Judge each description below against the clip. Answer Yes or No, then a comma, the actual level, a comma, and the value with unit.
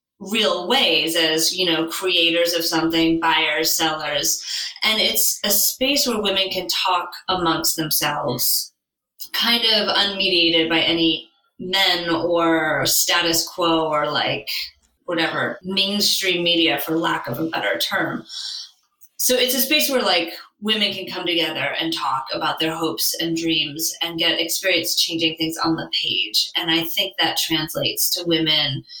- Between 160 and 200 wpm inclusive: No, average, 150 wpm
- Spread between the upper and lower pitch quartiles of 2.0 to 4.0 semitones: Yes, average, 3.0 semitones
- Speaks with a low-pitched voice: No, medium, 170 Hz